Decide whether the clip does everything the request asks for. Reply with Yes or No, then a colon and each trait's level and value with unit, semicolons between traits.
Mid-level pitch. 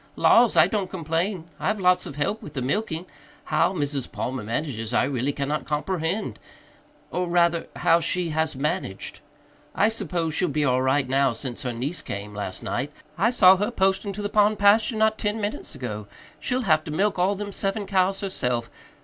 Yes: medium, 165 Hz